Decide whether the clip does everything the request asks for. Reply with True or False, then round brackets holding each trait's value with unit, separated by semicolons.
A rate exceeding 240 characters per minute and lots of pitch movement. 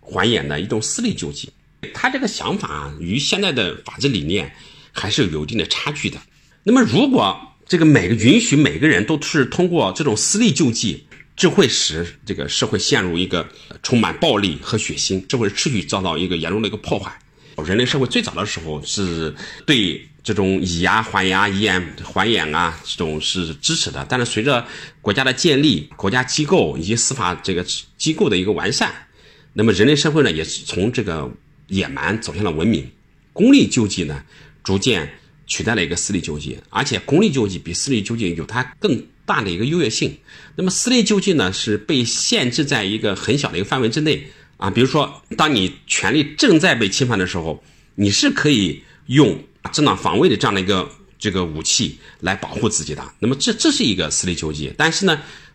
True (300 characters per minute; 8.4 semitones)